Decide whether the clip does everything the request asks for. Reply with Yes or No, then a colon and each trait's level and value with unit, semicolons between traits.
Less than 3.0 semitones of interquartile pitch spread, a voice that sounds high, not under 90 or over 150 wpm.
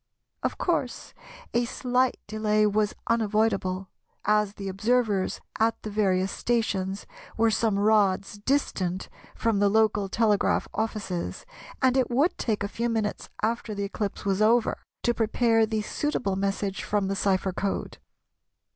Yes: narrow, 2.5 semitones; high, 210 Hz; average, 140 wpm